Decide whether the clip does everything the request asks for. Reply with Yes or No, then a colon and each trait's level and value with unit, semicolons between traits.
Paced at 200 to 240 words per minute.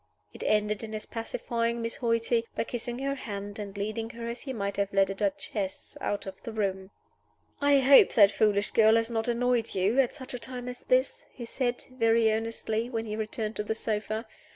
Yes: fast, 205 wpm